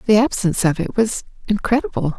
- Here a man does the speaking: No, female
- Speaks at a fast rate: No, average, 165 wpm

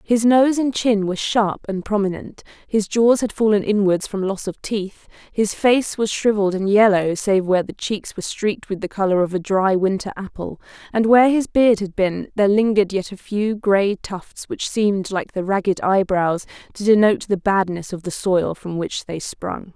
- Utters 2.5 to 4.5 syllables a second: No, 5.0 syllables/s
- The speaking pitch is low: No, high, 200 Hz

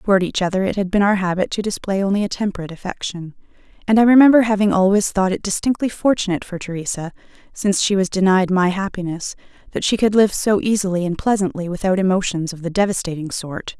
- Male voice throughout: No, female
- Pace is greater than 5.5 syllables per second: Yes, 6.5 syllables/s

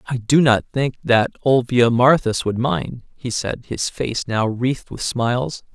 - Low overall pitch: Yes, low, 120 Hz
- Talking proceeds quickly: No, average, 175 wpm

